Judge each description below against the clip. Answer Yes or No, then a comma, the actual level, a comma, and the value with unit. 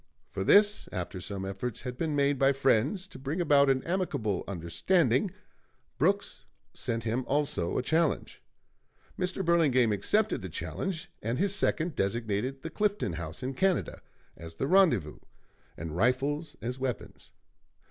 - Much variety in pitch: Yes, wide, 7.9 semitones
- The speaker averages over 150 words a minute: No, average, 145 wpm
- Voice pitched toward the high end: No, low, 135 Hz